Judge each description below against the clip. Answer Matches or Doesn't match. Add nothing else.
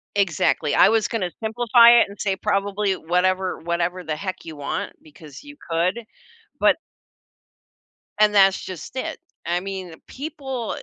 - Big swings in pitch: Doesn't match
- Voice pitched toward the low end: Doesn't match